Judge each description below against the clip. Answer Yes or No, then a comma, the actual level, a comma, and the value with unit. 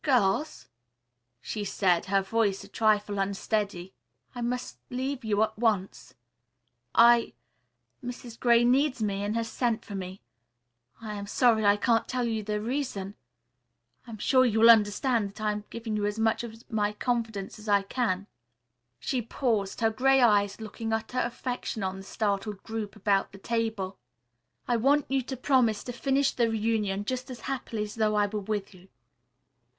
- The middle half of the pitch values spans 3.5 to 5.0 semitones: No, average, 2.9 semitones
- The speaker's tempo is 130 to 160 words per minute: No, average, 170 wpm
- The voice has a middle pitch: No, high, 220 Hz